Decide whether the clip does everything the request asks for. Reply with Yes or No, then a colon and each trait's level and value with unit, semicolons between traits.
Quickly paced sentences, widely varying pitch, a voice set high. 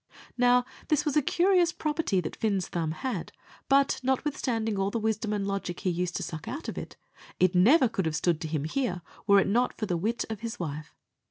Yes: fast, 220 wpm; wide, 6.4 semitones; high, 215 Hz